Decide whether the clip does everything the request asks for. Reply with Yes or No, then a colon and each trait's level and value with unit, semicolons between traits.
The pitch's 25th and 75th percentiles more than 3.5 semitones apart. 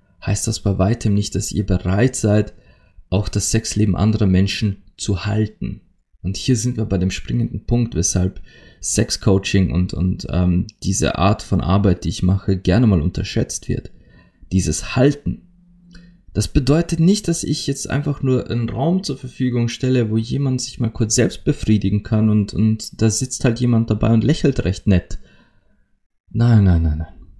Yes: average, 4.6 semitones